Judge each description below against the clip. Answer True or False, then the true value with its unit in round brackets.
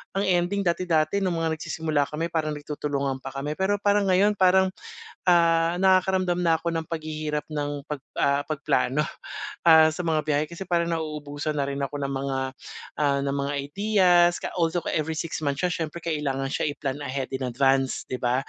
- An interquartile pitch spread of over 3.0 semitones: True (3.4 semitones)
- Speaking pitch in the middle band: True (155 Hz)